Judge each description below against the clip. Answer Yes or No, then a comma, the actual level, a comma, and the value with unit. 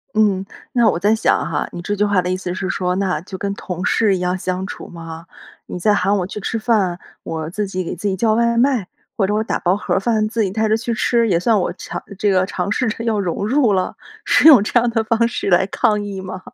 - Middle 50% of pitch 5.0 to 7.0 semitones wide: No, average, 3.2 semitones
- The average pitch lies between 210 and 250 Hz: No, high, 200 Hz